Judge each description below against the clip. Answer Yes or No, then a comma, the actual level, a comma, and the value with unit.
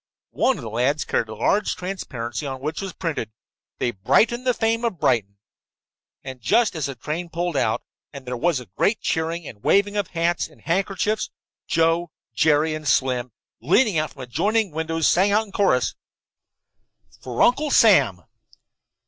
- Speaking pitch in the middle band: Yes, medium, 160 Hz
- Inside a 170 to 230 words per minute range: No, average, 160 wpm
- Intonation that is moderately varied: No, wide, 7.3 semitones